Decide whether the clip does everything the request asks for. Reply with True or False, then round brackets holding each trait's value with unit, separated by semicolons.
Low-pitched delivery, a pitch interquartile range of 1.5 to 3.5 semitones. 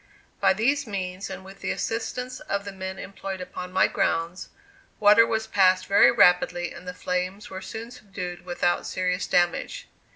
False (190 Hz; 2.7 semitones)